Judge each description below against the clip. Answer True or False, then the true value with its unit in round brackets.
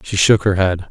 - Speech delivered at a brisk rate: True (265 wpm)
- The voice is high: False (95 Hz)